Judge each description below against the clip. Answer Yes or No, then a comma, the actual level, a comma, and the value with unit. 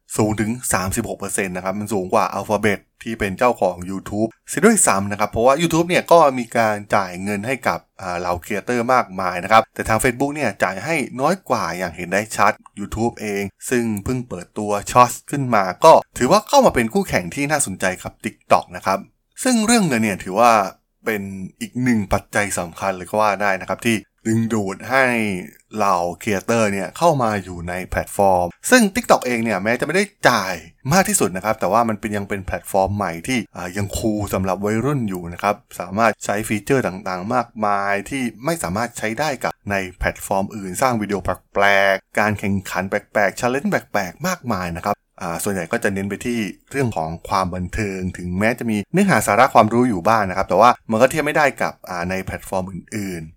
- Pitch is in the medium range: No, low, 105 Hz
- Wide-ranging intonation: No, average, 4.2 semitones